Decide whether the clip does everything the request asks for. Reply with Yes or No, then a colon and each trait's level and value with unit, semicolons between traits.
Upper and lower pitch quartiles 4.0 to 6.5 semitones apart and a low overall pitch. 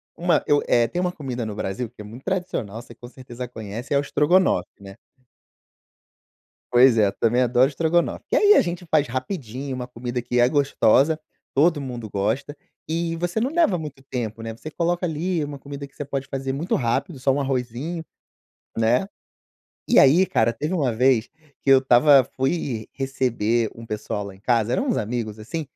Yes: average, 4.9 semitones; low, 130 Hz